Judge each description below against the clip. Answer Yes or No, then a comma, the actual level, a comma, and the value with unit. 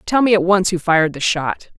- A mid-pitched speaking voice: Yes, medium, 180 Hz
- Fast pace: Yes, fast, 270 wpm